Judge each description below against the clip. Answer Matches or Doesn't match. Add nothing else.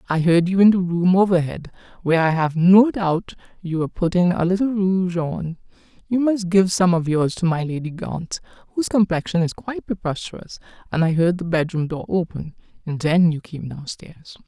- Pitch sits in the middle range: Matches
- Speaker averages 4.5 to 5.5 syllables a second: Matches